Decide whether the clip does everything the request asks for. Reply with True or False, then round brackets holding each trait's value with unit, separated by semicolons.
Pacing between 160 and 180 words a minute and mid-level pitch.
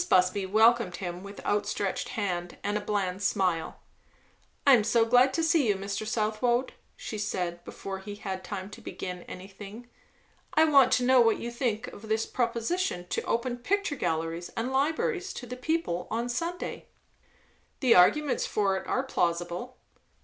False (165 wpm; 215 Hz)